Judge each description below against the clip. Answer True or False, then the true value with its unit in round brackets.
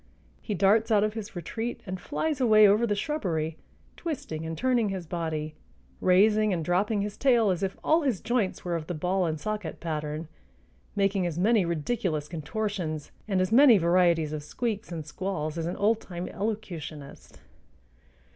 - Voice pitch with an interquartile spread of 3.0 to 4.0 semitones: False (4.8 semitones)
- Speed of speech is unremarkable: True (170 wpm)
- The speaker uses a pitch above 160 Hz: True (190 Hz)